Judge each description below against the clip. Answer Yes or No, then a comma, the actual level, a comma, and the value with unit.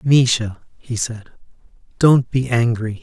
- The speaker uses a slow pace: Yes, slow, 120 wpm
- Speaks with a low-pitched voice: Yes, low, 120 Hz